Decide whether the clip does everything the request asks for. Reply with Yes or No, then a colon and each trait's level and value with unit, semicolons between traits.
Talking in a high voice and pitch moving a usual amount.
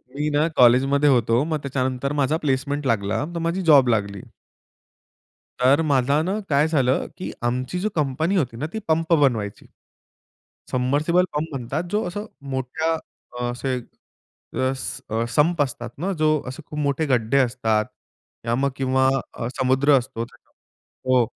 No: low, 135 Hz; average, 3.6 semitones